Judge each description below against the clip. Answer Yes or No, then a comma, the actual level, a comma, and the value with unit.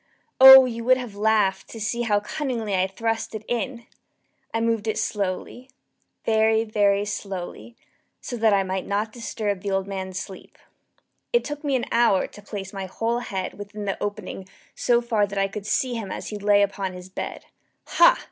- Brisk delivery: No, average, 185 wpm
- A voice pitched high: Yes, high, 210 Hz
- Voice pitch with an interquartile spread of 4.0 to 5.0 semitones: No, average, 2.8 semitones